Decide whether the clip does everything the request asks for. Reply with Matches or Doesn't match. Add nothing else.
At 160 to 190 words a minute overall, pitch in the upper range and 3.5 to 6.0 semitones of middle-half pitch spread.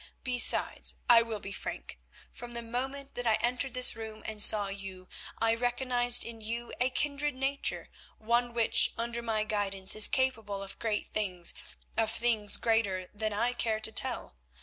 Doesn't match